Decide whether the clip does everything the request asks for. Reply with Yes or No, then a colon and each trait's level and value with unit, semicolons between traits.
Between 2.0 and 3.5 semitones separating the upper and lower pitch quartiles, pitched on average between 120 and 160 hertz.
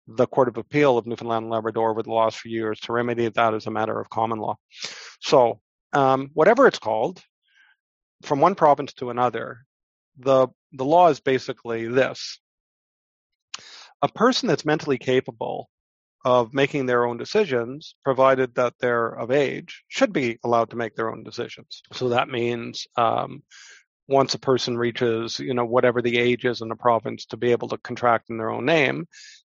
Yes: average, 2.9 semitones; low, 125 Hz